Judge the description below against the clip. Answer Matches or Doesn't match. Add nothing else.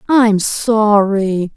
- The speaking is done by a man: Doesn't match